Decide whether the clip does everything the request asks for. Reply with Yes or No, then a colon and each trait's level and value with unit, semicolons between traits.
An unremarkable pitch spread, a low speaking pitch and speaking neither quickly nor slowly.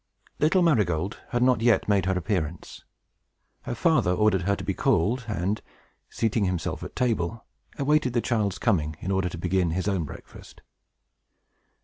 Yes: average, 4.6 semitones; low, 100 Hz; average, 155 wpm